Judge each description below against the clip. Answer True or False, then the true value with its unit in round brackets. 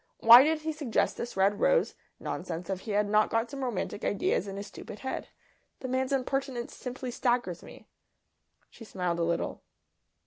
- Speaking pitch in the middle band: False (235 Hz)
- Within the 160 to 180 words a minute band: True (175 wpm)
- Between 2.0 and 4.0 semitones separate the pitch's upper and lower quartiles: False (4.9 semitones)